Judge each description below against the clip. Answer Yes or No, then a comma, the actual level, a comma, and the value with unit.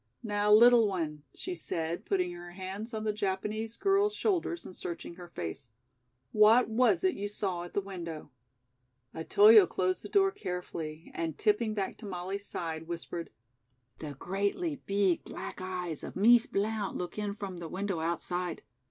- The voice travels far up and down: No, average, 3.8 semitones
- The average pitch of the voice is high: Yes, high, 195 Hz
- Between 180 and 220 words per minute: No, average, 160 wpm